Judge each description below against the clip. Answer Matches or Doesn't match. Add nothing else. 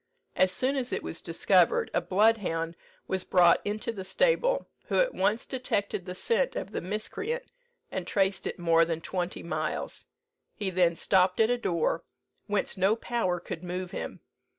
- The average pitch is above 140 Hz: Matches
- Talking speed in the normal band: Matches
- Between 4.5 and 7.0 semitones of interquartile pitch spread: Matches